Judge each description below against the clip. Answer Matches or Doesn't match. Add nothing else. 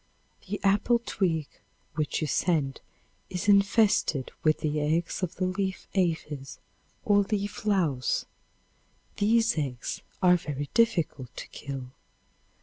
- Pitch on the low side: Doesn't match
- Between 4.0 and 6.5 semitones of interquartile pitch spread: Matches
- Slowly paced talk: Matches